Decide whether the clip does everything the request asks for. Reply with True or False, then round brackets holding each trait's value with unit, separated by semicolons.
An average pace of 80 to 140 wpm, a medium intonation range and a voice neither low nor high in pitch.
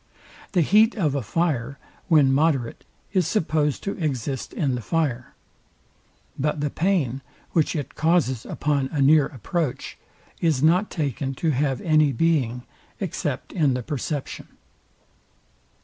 True (135 wpm; 3.6 semitones; 150 Hz)